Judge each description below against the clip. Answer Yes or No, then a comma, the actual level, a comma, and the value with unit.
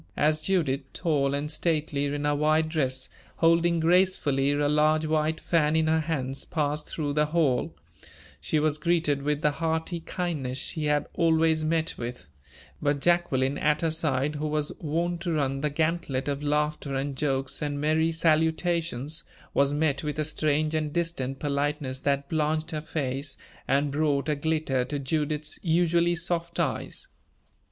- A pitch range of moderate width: No, narrow, 2.1 semitones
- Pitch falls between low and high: Yes, medium, 150 Hz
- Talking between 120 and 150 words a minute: No, average, 160 wpm